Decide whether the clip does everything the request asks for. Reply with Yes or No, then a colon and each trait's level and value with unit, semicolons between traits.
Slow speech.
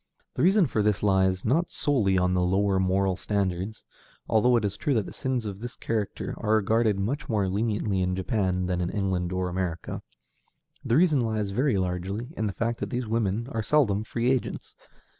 No: average, 190 wpm